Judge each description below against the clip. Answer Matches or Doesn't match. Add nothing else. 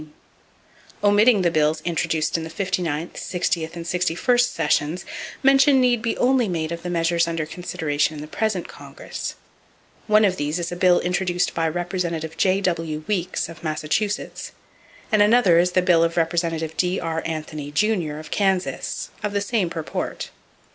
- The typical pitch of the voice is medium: Matches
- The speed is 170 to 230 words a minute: Doesn't match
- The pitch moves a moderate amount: Matches